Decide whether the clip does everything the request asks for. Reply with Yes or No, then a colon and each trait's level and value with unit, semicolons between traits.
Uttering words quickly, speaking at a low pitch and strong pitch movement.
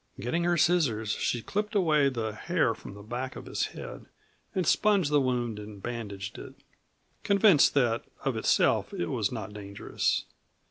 No: average, 165 wpm; low, 125 Hz; wide, 7.9 semitones